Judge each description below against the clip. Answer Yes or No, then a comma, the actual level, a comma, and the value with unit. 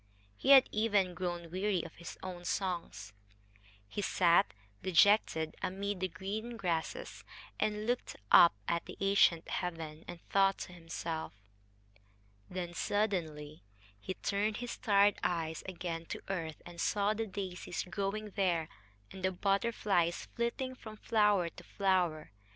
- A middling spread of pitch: Yes, average, 3.4 semitones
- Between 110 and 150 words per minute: Yes, slow, 135 wpm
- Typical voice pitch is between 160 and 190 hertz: Yes, medium, 185 Hz